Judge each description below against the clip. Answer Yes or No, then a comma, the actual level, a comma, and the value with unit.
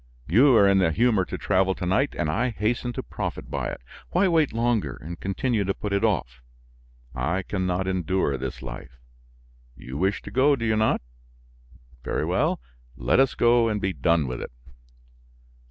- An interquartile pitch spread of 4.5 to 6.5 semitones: Yes, average, 5.3 semitones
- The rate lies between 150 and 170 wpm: No, average, 185 wpm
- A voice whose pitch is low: Yes, very low, 95 Hz